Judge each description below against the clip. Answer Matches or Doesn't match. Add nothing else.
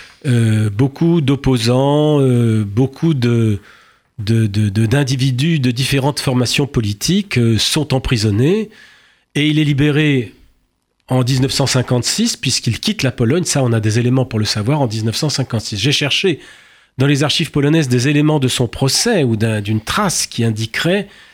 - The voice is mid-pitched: Doesn't match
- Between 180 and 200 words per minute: Doesn't match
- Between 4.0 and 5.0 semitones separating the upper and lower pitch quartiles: Matches